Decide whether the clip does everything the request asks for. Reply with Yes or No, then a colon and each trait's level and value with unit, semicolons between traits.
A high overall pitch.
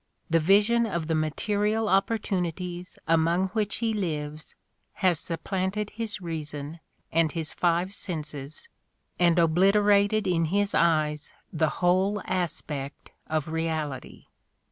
No: medium, 175 Hz